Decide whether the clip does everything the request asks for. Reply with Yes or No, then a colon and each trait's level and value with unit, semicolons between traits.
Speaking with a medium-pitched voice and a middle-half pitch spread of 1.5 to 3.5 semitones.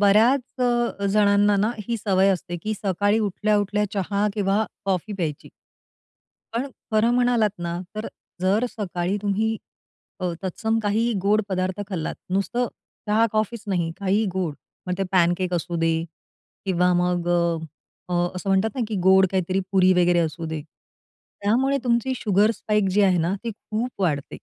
No: high, 195 Hz; average, 3.1 semitones